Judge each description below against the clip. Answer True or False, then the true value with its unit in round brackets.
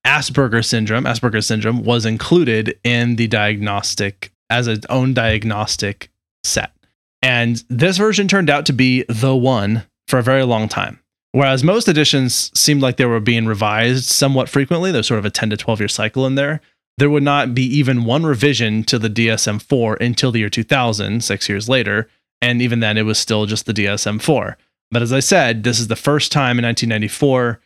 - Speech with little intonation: False (3.2 semitones)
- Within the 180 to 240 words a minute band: True (190 wpm)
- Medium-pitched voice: False (120 Hz)